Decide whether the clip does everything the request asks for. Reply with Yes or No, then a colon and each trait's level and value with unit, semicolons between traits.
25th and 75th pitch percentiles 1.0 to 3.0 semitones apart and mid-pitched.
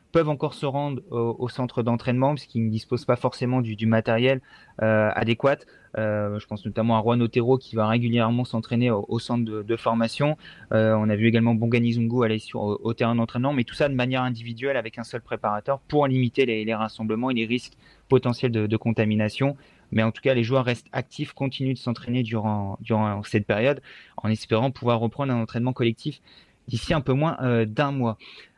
No: average, 2.7 semitones; low, 120 Hz